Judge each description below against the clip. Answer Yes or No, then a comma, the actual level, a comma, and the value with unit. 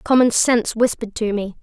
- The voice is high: Yes, high, 225 Hz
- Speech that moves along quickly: No, average, 185 wpm